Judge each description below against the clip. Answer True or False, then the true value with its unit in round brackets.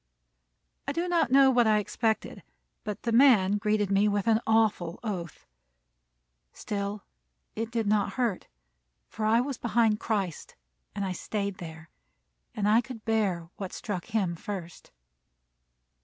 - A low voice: False (210 Hz)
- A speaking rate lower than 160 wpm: True (140 wpm)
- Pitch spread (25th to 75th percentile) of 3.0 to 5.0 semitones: False (2.6 semitones)